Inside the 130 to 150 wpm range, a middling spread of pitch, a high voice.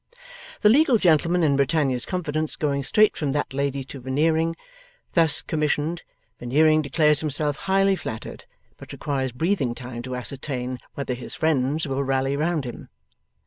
No: average, 145 wpm; average, 3.4 semitones; medium, 145 Hz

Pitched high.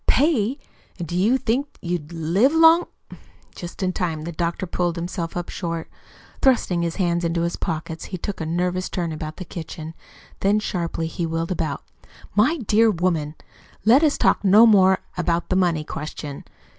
No: medium, 175 Hz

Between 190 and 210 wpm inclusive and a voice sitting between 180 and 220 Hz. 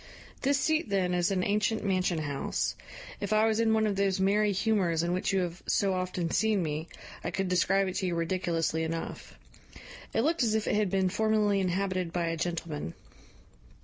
Yes: average, 195 wpm; high, 190 Hz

